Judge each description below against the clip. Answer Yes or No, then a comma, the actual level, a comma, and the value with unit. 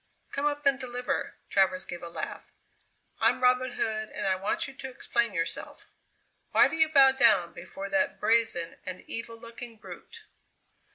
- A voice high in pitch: Yes, high, 235 Hz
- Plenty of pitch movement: Yes, wide, 5.8 semitones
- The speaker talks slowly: No, average, 165 wpm